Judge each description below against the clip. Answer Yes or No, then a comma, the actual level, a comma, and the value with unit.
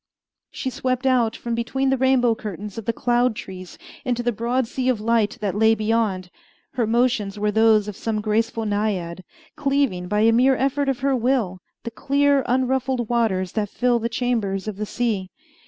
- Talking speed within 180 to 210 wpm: Yes, average, 185 wpm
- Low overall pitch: No, high, 230 Hz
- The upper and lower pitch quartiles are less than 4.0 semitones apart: Yes, average, 3.4 semitones